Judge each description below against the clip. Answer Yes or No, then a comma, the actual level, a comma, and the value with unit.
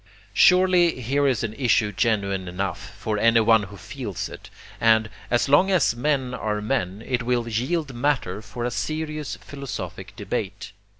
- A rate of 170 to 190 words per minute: No, average, 155 wpm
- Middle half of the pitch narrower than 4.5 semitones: No, average, 4.9 semitones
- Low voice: Yes, low, 115 Hz